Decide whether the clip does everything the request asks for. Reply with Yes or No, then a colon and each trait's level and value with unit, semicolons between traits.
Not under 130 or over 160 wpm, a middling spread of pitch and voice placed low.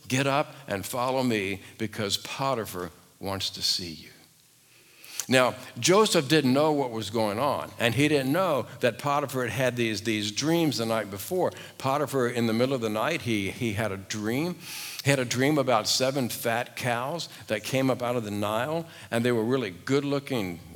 No: average, 190 wpm; average, 4.1 semitones; low, 125 Hz